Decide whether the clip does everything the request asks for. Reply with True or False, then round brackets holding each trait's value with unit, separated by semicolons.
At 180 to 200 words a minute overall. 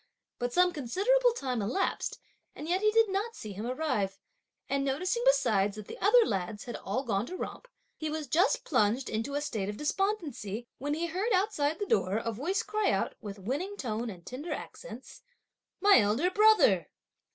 True (185 wpm)